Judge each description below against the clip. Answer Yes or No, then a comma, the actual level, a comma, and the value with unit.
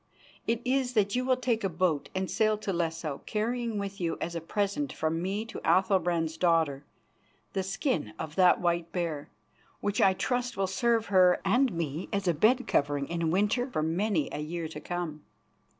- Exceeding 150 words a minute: Yes, average, 185 wpm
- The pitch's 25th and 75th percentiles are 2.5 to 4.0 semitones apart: No, average, 4.7 semitones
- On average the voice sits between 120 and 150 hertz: No, medium, 185 Hz